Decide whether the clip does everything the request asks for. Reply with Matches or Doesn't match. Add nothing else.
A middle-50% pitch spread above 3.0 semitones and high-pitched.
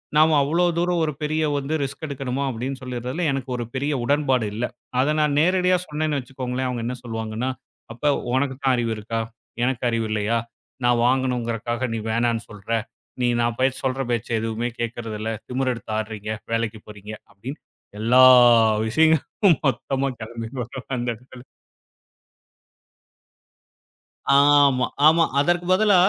Doesn't match